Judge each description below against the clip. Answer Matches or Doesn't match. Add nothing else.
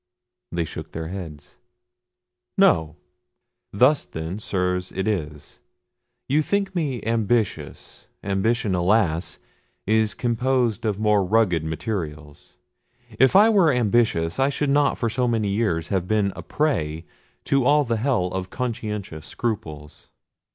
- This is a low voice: Matches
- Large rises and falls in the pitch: Matches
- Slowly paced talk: Matches